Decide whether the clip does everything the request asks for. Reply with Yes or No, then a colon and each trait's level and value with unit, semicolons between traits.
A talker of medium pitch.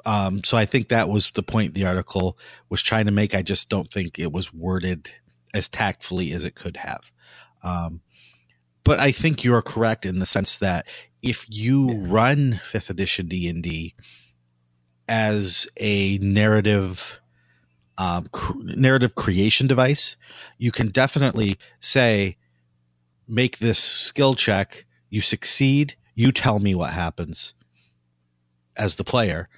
No: low, 100 Hz